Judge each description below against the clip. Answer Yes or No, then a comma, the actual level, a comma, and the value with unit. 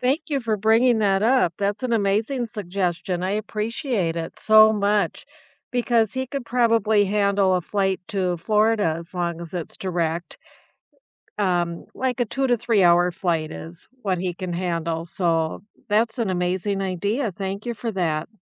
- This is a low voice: No, high, 200 Hz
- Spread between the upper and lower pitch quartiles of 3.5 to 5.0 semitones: Yes, average, 4.2 semitones